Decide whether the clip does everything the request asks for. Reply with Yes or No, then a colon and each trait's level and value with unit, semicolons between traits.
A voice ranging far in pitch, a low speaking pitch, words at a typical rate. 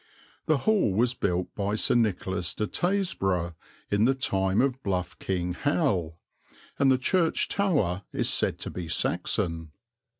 Yes: wide, 7.0 semitones; low, 100 Hz; average, 145 wpm